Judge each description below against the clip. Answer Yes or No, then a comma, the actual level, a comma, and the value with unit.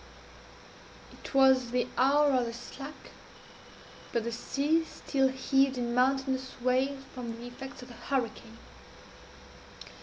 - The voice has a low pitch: No, very high, 260 Hz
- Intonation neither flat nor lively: No, narrow, 1.9 semitones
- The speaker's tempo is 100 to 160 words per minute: Yes, average, 140 wpm